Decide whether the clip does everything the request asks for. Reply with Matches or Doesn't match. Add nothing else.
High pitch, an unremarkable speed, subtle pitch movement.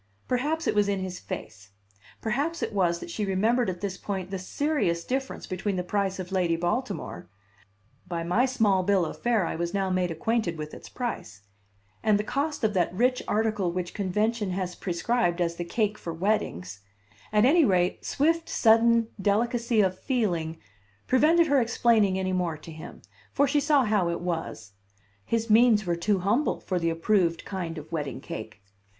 Doesn't match